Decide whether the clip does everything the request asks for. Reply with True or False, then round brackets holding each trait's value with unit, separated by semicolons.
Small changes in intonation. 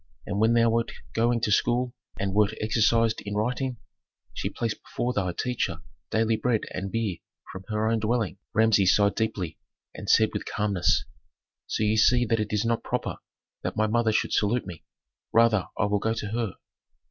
True (2.1 semitones)